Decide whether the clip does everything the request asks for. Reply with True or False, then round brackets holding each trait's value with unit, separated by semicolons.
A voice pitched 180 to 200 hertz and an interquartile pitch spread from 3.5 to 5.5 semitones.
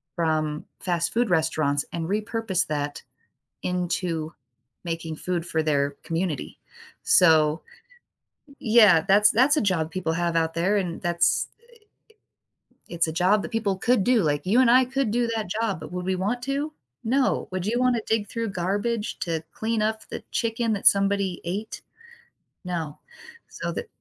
True (185 Hz; 5.2 semitones)